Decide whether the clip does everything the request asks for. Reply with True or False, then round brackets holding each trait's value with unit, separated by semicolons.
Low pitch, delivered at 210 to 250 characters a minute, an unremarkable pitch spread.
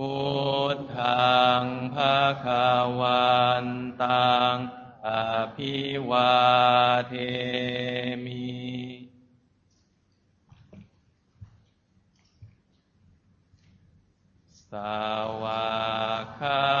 False (125 Hz; 95 characters per minute; 3.2 semitones)